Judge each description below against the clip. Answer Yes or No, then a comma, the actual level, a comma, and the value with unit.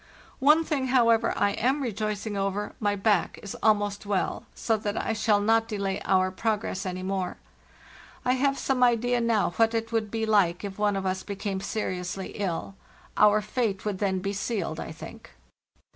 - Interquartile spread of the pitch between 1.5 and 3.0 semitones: Yes, narrow, 2.6 semitones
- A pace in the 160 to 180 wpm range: Yes, average, 175 wpm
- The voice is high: Yes, high, 210 Hz